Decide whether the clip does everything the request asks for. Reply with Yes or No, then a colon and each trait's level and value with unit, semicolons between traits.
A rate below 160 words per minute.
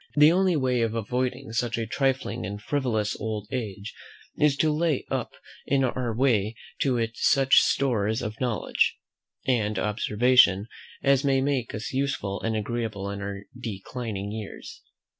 Yes: average, 150 wpm